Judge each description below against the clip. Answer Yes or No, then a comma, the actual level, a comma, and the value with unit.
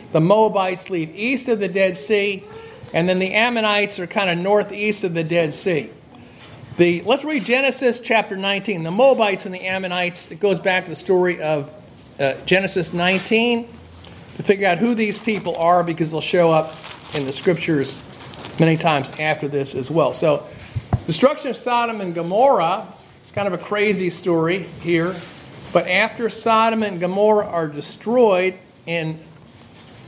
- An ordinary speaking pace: Yes, average, 165 wpm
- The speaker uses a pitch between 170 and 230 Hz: Yes, medium, 185 Hz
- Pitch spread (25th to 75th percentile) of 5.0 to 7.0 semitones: No, average, 4.3 semitones